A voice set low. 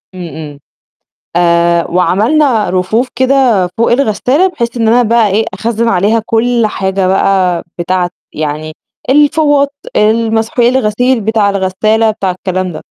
No: high, 215 Hz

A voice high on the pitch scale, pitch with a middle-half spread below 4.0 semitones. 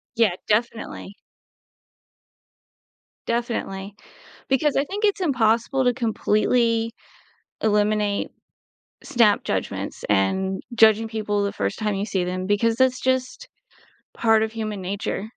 Yes: high, 220 Hz; average, 2.9 semitones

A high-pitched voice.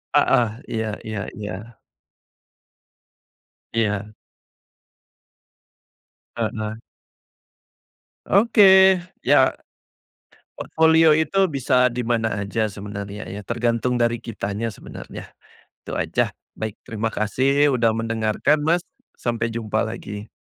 No: low, 115 Hz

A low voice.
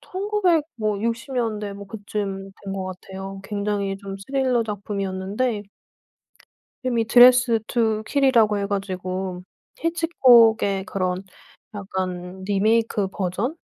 No: high, 210 Hz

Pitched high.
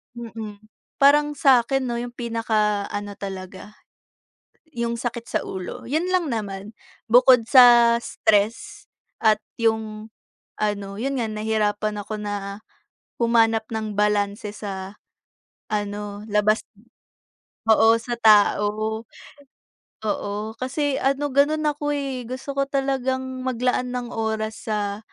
Yes: high, 225 Hz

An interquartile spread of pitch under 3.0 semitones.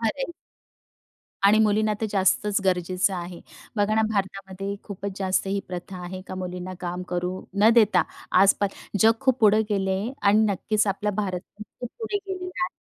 Yes: narrow, 2.6 semitones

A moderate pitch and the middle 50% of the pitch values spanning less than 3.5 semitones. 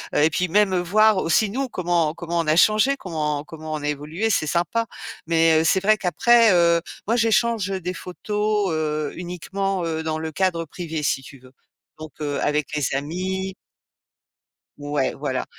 No: medium, 170 Hz; average, 4.2 semitones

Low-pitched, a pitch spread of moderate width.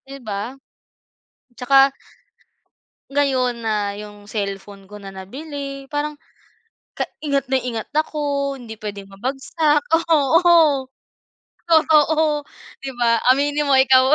No: very high, 270 Hz; average, 5.0 semitones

